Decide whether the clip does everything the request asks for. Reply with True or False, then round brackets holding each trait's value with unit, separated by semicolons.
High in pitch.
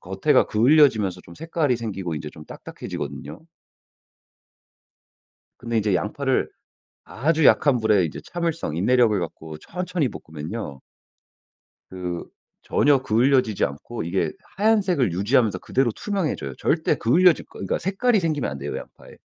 False (120 Hz)